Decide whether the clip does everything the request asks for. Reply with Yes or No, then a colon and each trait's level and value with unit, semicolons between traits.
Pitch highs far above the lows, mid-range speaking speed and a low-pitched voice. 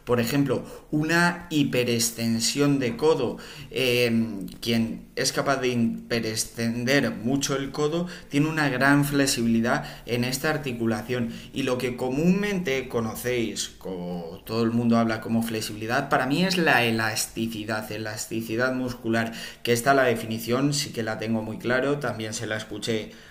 No: average, 3.7 semitones; average, 140 wpm; low, 120 Hz